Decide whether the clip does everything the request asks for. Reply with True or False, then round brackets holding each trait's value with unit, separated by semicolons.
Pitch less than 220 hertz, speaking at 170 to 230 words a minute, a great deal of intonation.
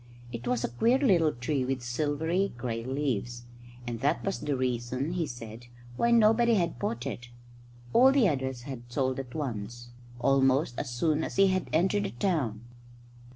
True (135 Hz; 175 wpm; 5.9 semitones)